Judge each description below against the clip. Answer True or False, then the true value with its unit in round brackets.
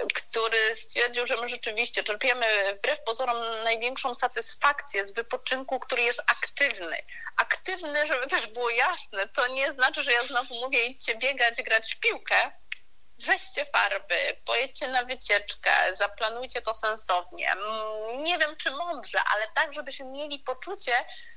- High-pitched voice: True (245 Hz)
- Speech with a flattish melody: False (4.3 semitones)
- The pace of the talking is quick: False (140 wpm)